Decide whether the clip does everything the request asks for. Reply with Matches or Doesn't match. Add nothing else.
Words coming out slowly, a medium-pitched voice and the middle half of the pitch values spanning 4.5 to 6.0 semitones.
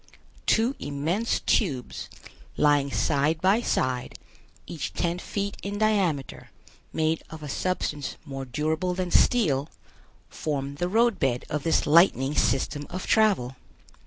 Matches